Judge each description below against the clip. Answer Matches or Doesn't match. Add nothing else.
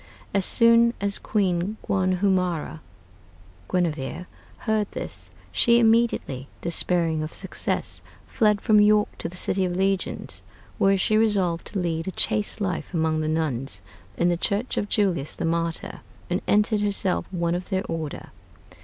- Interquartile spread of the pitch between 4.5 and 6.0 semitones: Doesn't match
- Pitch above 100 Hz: Matches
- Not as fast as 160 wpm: Matches